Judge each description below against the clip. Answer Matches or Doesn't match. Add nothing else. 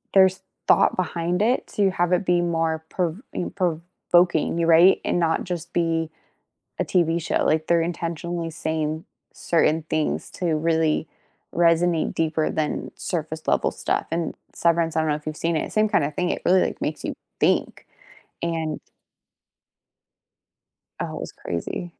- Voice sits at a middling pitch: Matches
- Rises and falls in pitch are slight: Matches